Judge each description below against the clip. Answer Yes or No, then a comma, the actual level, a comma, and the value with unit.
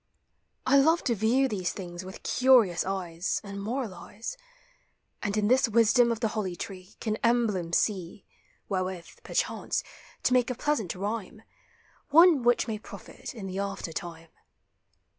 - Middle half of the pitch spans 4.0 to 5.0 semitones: Yes, average, 4.5 semitones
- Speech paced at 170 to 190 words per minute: No, average, 145 wpm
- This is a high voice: Yes, high, 210 Hz